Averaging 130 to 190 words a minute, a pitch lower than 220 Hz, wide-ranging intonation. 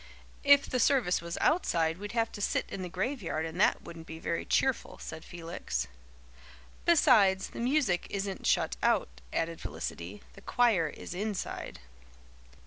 Yes: average, 150 wpm; high, 190 Hz; wide, 6.3 semitones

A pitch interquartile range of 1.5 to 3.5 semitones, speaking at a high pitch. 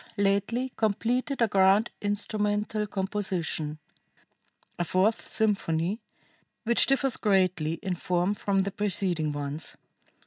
Yes: average, 3.0 semitones; high, 200 Hz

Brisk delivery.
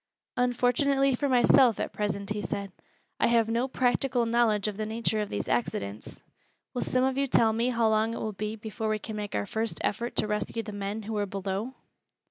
Yes: fast, 210 wpm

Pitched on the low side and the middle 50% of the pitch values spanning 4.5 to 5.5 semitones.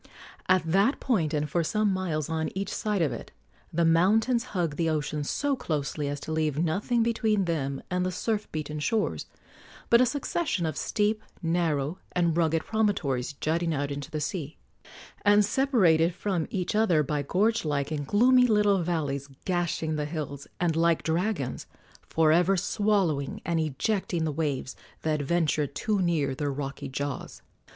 No: medium, 165 Hz; average, 5.2 semitones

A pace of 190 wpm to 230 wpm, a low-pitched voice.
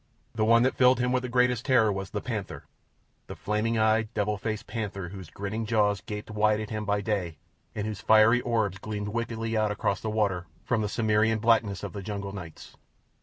Yes: average, 200 wpm; low, 110 Hz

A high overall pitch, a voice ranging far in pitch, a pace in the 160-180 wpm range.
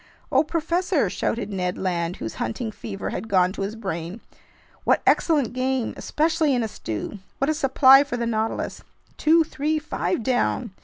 Yes: high, 235 Hz; wide, 7.1 semitones; average, 165 wpm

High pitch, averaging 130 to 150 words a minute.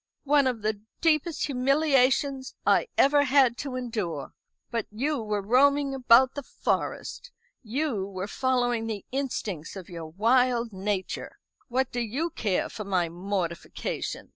Yes: high, 245 Hz; average, 140 wpm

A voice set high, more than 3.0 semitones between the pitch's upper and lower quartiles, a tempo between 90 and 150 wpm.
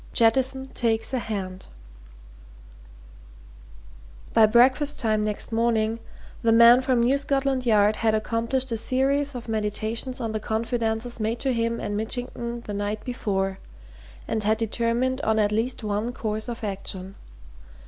No: high, 230 Hz; narrow, 2.4 semitones; average, 140 wpm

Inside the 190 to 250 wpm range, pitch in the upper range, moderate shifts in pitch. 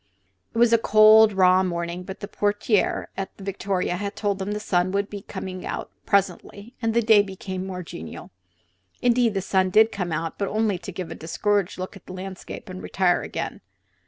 No: average, 195 wpm; high, 195 Hz; narrow, 2.2 semitones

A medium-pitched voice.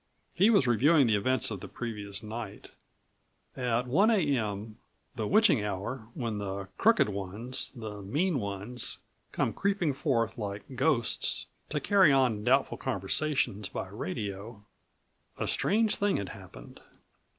No: low, 115 Hz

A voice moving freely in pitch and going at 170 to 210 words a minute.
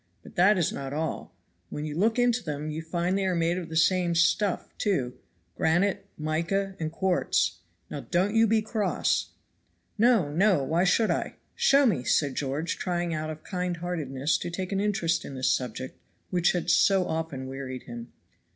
No: average, 4.1 semitones; average, 180 wpm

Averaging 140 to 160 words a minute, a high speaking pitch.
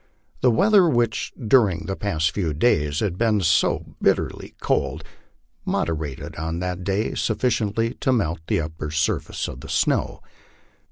No: average, 145 wpm; very low, 95 Hz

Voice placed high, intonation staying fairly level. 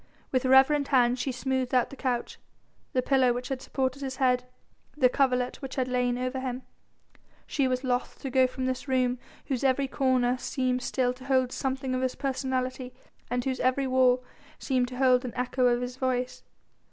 Yes: very high, 255 Hz; narrow, 0.9 semitones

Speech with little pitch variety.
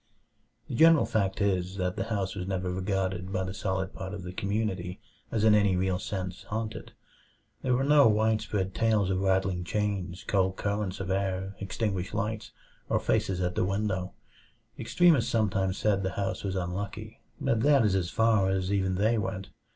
Yes: narrow, 2.3 semitones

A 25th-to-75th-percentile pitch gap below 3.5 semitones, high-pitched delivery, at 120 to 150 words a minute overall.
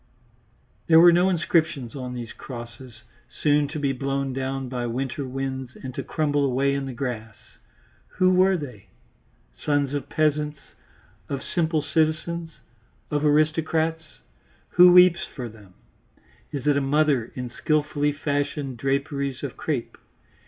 No: average, 3.0 semitones; medium, 145 Hz; average, 140 wpm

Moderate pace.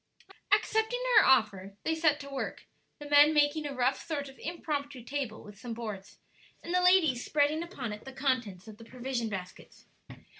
Yes: average, 180 wpm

